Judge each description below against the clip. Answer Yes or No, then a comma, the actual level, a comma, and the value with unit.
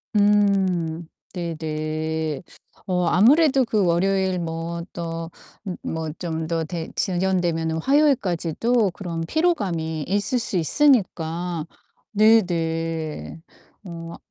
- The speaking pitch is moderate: Yes, medium, 175 Hz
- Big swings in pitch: No, average, 3.6 semitones